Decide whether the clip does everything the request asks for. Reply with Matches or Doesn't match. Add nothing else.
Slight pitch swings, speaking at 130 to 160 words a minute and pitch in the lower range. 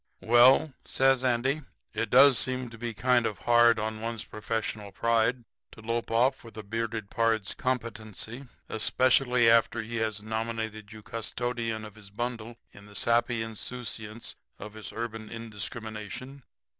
Matches